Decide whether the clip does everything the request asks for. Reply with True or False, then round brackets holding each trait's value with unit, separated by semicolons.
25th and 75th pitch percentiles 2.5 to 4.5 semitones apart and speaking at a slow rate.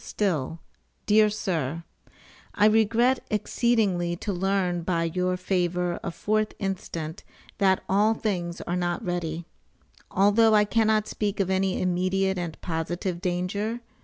True (3.2 semitones; 130 wpm)